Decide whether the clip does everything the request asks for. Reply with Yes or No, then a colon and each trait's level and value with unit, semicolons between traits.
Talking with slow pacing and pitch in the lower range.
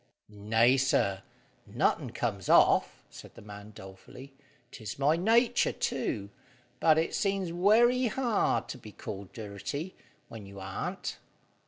Yes: slow, 130 wpm; low, 130 Hz